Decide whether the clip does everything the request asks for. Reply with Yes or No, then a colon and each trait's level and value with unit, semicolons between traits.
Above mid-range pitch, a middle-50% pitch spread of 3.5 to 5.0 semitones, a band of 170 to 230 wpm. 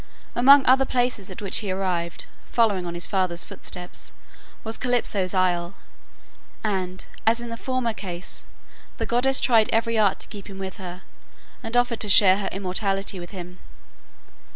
No: high, 195 Hz; average, 3.9 semitones; average, 160 wpm